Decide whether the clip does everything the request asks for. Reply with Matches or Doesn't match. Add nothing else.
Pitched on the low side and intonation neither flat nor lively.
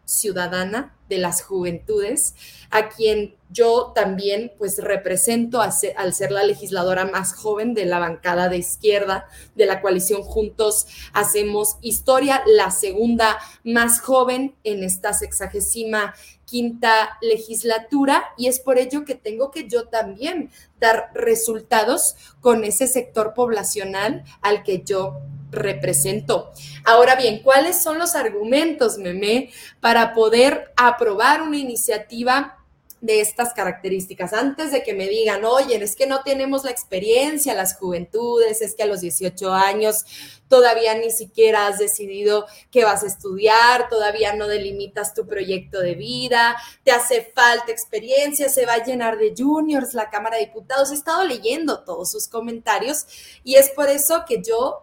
Doesn't match